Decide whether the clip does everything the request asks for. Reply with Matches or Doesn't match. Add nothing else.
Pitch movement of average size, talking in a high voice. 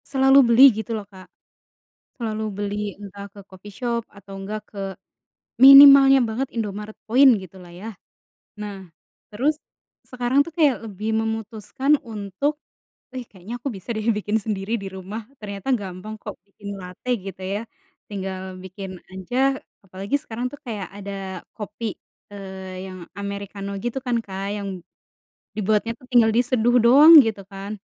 Matches